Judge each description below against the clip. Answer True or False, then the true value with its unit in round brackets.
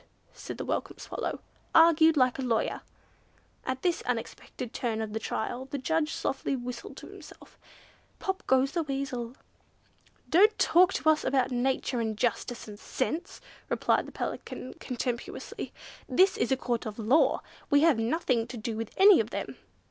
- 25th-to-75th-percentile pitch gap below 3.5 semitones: False (4.9 semitones)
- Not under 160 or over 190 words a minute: True (165 wpm)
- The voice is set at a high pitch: True (260 Hz)